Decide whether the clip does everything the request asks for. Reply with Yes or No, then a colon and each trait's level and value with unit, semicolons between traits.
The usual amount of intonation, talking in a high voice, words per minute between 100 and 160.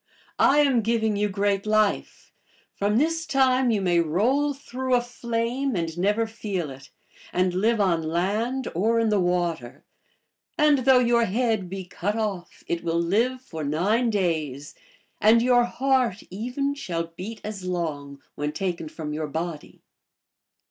No: wide, 5.8 semitones; high, 205 Hz; average, 155 wpm